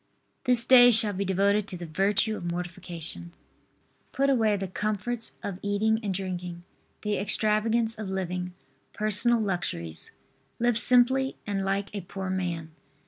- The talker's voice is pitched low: No, high, 200 Hz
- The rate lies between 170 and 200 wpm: No, average, 140 wpm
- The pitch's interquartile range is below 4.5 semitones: Yes, average, 3.3 semitones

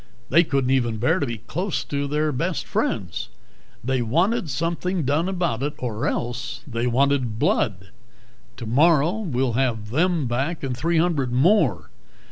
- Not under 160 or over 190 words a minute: No, average, 150 wpm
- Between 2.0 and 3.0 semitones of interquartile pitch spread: No, wide, 5.6 semitones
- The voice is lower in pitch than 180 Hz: Yes, medium, 140 Hz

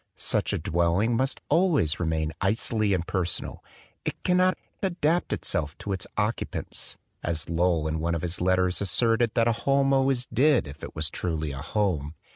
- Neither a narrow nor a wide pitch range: No, wide, 6.8 semitones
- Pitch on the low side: Yes, very low, 95 Hz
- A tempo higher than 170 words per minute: No, average, 160 wpm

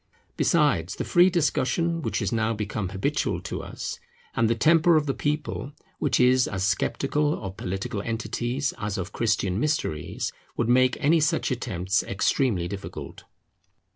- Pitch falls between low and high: No, low, 120 Hz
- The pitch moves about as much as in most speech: No, wide, 6.8 semitones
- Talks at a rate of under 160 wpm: Yes, average, 150 wpm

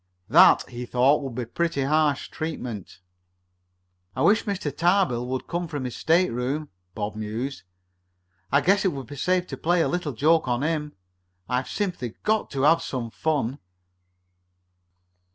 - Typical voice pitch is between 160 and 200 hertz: No, medium, 145 Hz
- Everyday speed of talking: Yes, average, 155 wpm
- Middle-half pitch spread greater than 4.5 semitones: Yes, average, 5.1 semitones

